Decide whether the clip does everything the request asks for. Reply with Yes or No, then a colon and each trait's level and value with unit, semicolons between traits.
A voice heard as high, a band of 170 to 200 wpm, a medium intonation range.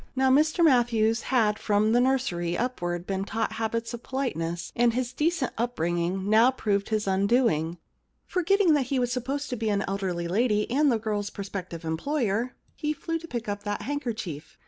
Yes: high, 225 Hz; average, 180 wpm; average, 4.7 semitones